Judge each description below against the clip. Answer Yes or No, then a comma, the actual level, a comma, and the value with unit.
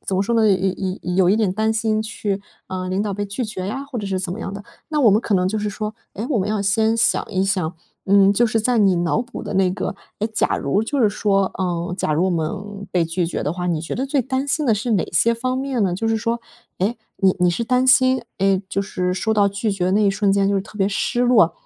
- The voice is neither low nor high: No, high, 200 Hz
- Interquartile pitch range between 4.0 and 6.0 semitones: No, average, 3.1 semitones